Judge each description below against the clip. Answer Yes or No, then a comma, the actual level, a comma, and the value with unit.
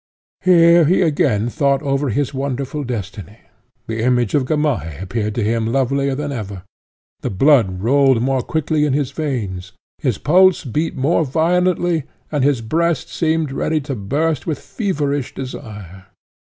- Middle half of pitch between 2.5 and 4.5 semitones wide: No, average, 5.1 semitones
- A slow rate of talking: No, average, 150 wpm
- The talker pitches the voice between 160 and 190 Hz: No, low, 135 Hz